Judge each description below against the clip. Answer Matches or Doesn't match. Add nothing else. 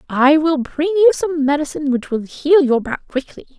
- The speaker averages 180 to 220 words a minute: Matches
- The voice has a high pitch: Matches